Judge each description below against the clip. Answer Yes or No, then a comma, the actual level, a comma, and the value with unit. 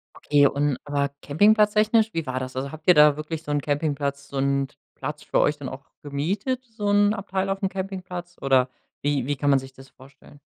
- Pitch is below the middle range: No, medium, 145 Hz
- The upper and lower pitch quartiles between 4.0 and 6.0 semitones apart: Yes, wide, 5.6 semitones